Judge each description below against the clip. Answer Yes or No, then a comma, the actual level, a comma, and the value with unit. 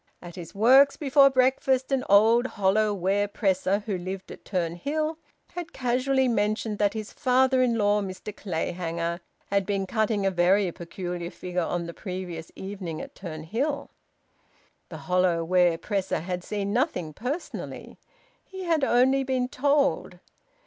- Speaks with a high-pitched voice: Yes, high, 205 Hz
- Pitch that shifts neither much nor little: No, wide, 6.0 semitones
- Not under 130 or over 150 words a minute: Yes, average, 145 wpm